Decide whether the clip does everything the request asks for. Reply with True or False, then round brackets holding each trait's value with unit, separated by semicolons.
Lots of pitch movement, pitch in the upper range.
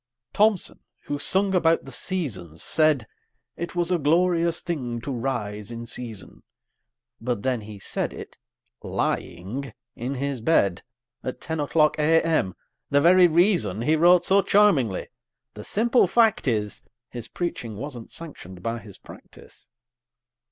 False (7.0 semitones; 140 Hz)